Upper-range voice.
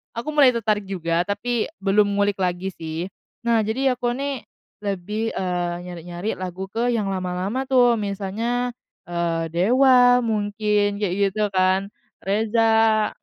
Yes: high, 205 Hz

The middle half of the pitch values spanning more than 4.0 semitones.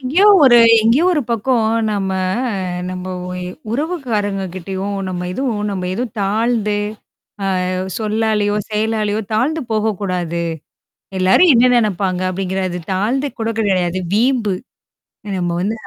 No: average, 3.7 semitones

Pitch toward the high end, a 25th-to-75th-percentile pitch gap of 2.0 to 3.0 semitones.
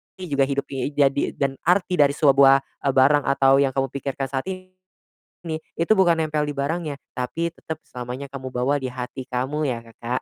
No: medium, 140 Hz; narrow, 2.6 semitones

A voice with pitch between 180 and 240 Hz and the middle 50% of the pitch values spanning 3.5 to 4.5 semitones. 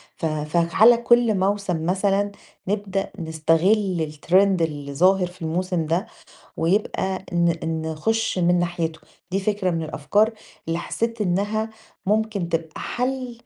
Yes: medium, 185 Hz; average, 4.1 semitones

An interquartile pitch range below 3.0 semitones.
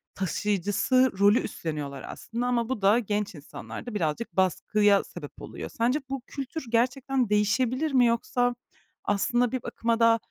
No: average, 3.7 semitones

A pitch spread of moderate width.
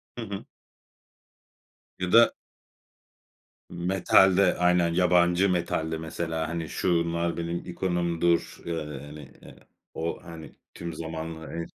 No: narrow, 1.6 semitones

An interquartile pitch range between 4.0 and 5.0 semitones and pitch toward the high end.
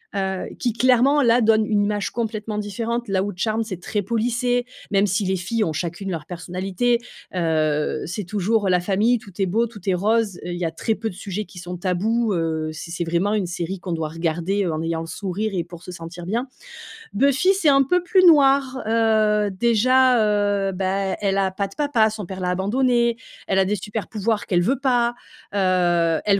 Yes: average, 4.3 semitones; high, 205 Hz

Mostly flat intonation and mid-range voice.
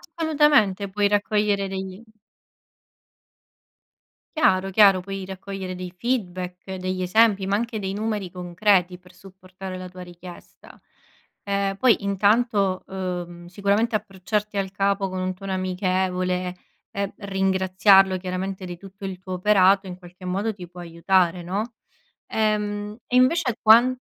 No: narrow, 2.0 semitones; high, 195 Hz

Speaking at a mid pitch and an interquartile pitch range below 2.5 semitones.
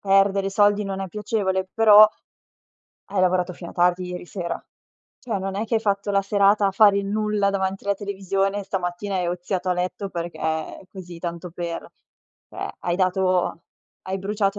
No: high, 195 Hz; narrow, 2.0 semitones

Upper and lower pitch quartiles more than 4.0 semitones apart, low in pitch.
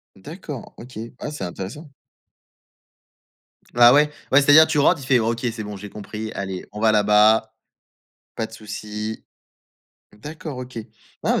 Yes: average, 4.9 semitones; low, 110 Hz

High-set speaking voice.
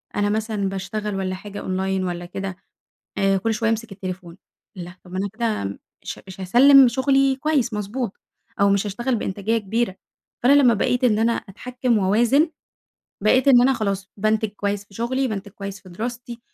Yes: high, 210 Hz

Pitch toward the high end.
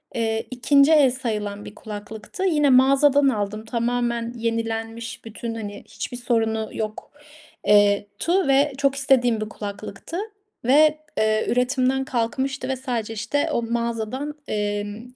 Yes: high, 235 Hz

